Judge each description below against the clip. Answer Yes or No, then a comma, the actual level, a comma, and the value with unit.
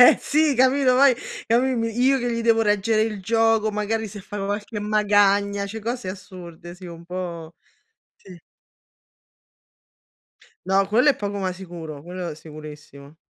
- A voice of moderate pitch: No, high, 205 Hz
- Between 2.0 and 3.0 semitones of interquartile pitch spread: No, average, 4.0 semitones